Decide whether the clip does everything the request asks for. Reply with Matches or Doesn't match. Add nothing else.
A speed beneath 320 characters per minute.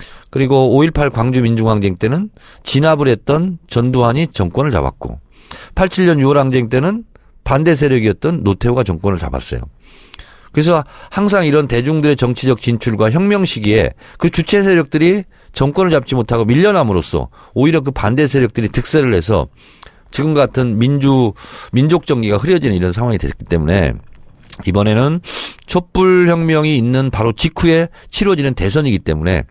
Doesn't match